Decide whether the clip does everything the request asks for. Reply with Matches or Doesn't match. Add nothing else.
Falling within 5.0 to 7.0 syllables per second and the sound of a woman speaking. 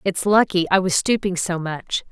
Doesn't match